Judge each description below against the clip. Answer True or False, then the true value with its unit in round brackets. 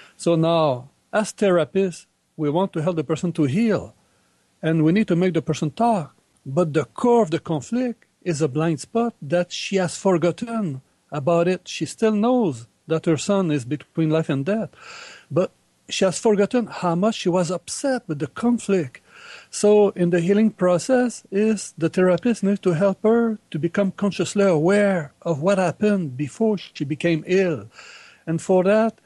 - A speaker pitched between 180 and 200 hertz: True (185 Hz)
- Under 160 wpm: False (175 wpm)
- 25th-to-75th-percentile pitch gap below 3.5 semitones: False (4.5 semitones)